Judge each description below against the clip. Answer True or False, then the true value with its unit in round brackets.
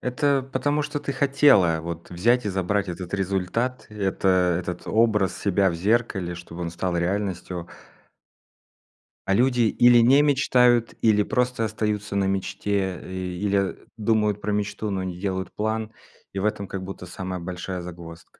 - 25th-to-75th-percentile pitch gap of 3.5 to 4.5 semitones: True (3.8 semitones)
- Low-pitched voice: True (100 Hz)